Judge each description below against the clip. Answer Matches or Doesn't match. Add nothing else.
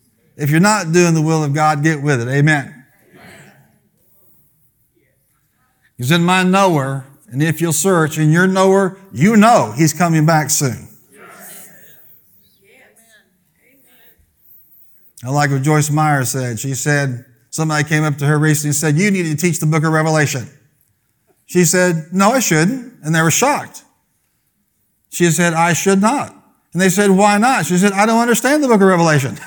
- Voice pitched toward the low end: Doesn't match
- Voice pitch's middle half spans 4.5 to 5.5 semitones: Doesn't match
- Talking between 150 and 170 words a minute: Matches